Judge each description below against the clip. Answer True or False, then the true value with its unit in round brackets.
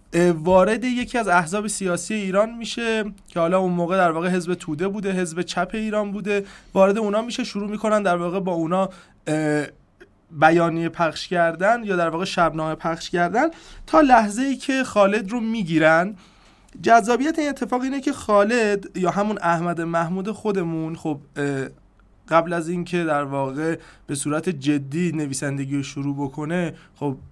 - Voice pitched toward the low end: False (180 Hz)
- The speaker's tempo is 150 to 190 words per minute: True (155 wpm)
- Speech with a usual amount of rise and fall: True (4.5 semitones)